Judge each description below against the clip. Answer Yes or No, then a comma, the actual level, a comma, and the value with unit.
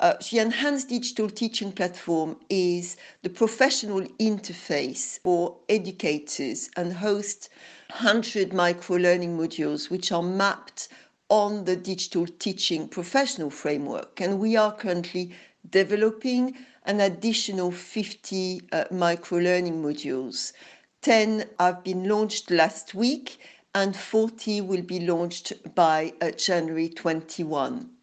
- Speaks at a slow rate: Yes, slow, 115 wpm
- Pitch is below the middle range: No, high, 190 Hz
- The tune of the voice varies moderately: Yes, average, 3.6 semitones